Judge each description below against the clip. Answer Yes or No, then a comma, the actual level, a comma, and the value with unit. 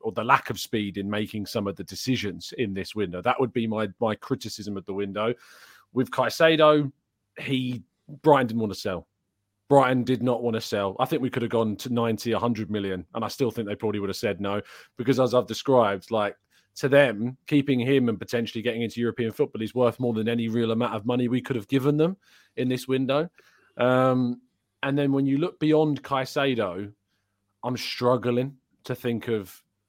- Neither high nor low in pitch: No, low, 120 Hz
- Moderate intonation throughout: Yes, average, 3.7 semitones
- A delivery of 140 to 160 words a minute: No, fast, 205 wpm